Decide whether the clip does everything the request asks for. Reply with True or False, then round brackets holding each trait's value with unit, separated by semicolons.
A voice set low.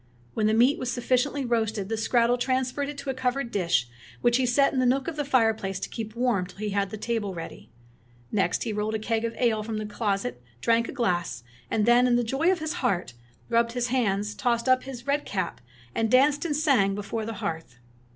False (230 Hz)